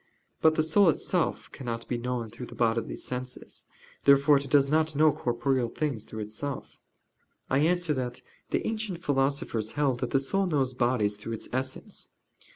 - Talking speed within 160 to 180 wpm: Yes, average, 165 wpm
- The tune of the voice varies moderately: Yes, average, 4.0 semitones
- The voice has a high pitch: No, low, 135 Hz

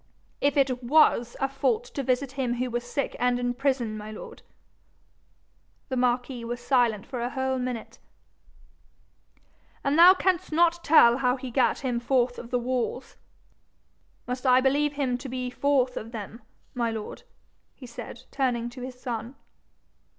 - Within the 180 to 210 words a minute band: No, average, 160 wpm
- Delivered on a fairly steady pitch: Yes, narrow, 2.1 semitones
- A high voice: Yes, very high, 250 Hz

